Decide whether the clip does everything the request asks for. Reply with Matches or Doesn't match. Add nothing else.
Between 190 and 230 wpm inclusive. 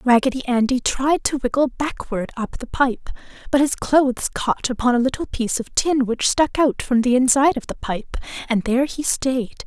Matches